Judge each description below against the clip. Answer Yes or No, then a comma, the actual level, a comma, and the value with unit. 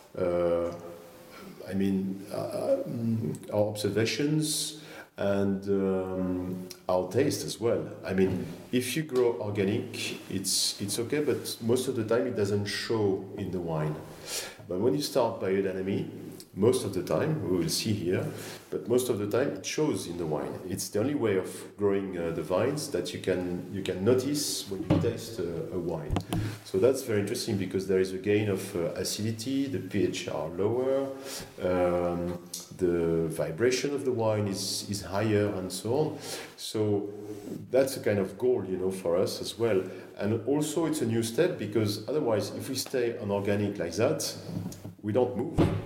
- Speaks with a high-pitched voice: No, low, 100 Hz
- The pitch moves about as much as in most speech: Yes, average, 3.7 semitones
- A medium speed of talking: Yes, average, 175 wpm